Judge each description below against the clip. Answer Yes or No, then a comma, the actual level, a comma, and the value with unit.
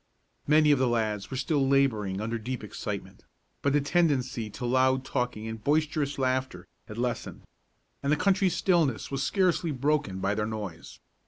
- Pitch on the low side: Yes, low, 130 Hz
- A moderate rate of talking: Yes, average, 165 wpm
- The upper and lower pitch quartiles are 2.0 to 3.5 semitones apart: No, average, 4.8 semitones